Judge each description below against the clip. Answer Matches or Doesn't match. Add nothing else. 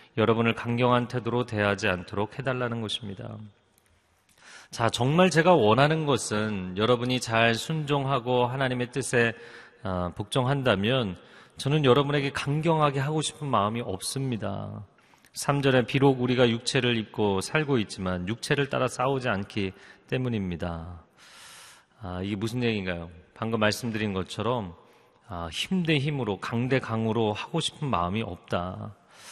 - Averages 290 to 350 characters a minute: Matches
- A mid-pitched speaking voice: Doesn't match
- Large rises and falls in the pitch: Doesn't match